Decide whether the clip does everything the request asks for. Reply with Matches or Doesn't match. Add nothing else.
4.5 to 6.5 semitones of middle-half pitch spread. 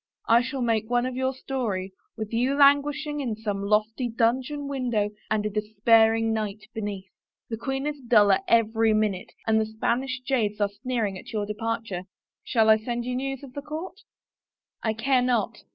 Doesn't match